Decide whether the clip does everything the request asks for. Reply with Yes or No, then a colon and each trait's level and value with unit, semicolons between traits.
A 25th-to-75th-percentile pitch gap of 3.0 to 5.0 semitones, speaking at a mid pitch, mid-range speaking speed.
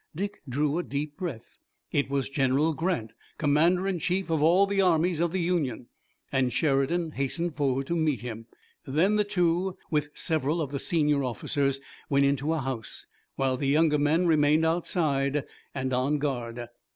Yes: average, 3.7 semitones; medium, 150 Hz; average, 170 wpm